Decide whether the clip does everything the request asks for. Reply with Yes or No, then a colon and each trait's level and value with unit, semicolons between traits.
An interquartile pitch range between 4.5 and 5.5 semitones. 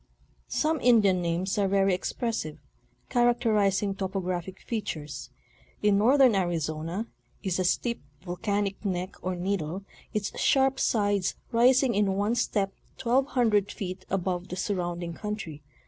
No: average, 3.7 semitones